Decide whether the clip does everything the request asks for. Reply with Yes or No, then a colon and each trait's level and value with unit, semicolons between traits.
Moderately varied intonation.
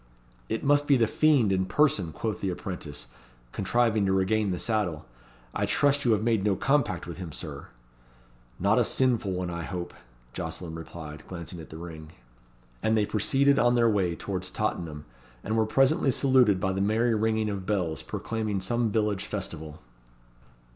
Yes: average, 4.4 semitones